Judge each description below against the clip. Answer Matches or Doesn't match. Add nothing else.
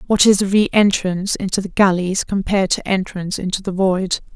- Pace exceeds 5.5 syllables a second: Matches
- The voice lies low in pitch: Doesn't match